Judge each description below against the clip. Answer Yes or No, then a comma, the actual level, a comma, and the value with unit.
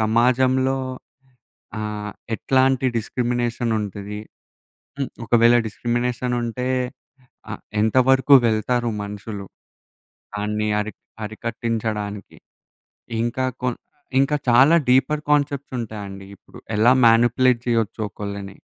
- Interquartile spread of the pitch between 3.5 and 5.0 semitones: No, average, 3.1 semitones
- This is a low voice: Yes, low, 115 Hz